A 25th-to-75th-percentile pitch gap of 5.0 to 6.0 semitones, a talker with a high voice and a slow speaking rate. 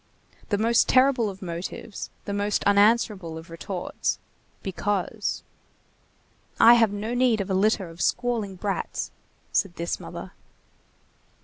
No: average, 3.3 semitones; high, 205 Hz; slow, 120 wpm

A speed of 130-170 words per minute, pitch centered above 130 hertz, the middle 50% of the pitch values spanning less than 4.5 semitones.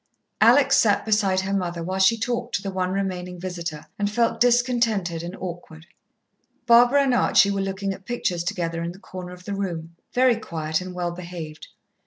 No: average, 185 wpm; medium, 185 Hz; average, 3.5 semitones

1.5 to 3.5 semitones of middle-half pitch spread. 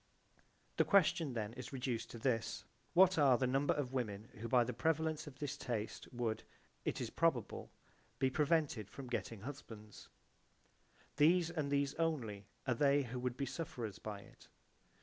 No: average, 4.3 semitones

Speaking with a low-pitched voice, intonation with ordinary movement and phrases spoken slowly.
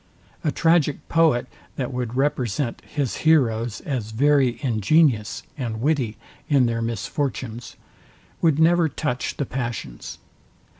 Yes: low, 130 Hz; average, 4.2 semitones; slow, 115 wpm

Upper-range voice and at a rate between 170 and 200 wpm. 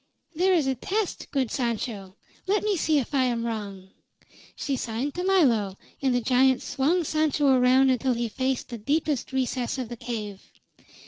Yes: very high, 260 Hz; average, 175 wpm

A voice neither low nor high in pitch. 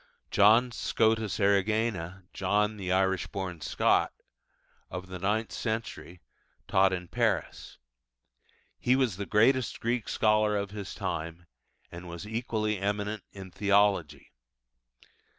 No: low, 100 Hz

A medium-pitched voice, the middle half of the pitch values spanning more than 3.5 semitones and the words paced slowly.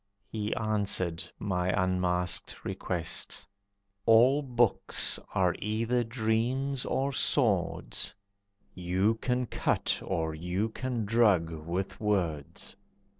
No: low, 105 Hz; average, 4.6 semitones; slow, 95 wpm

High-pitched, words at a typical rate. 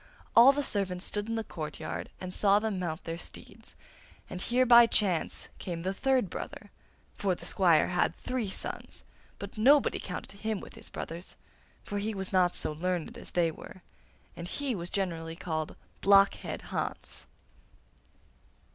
Yes: high, 195 Hz; average, 160 wpm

